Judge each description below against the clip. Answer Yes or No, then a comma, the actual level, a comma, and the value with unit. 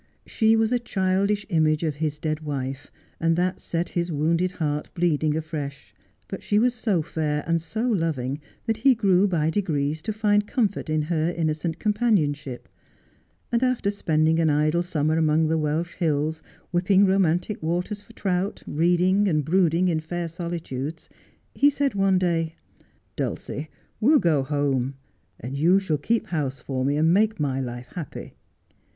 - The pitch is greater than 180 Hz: No, medium, 165 Hz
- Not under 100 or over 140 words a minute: No, average, 165 wpm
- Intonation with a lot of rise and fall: No, average, 4.3 semitones